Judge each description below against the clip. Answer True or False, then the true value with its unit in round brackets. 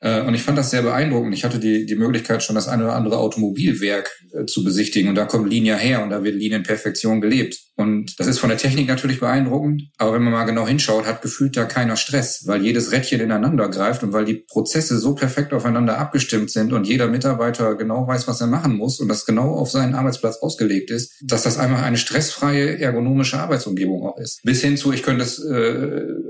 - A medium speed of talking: False (215 wpm)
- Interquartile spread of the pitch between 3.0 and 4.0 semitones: True (3.3 semitones)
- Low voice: True (120 Hz)